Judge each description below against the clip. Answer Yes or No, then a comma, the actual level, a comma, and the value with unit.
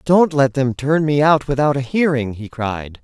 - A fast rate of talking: Yes, fast, 215 wpm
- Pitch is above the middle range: No, medium, 140 Hz